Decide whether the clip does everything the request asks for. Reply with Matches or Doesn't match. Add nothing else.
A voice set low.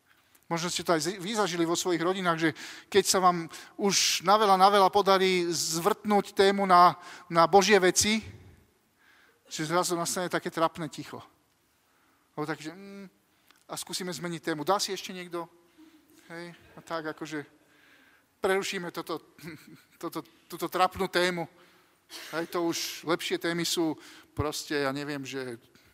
Doesn't match